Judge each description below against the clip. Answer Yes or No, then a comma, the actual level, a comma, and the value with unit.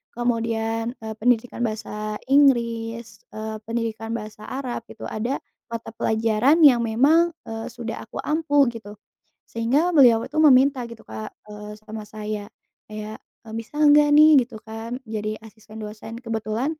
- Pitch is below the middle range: No, high, 230 Hz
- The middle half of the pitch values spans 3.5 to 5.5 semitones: No, average, 2.7 semitones